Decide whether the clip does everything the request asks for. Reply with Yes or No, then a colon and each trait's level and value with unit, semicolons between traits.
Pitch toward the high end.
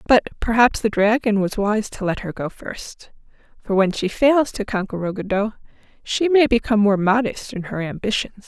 Yes: high, 215 Hz